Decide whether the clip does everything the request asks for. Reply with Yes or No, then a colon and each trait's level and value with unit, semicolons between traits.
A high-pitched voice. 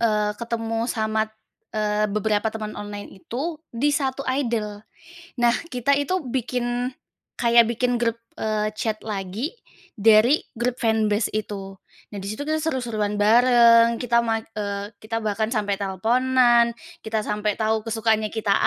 Yes: high, 225 Hz